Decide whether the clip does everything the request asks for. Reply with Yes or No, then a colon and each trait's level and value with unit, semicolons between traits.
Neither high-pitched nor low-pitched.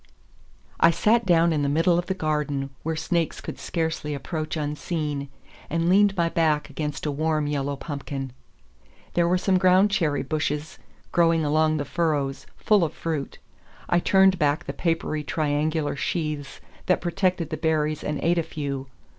Yes: medium, 155 Hz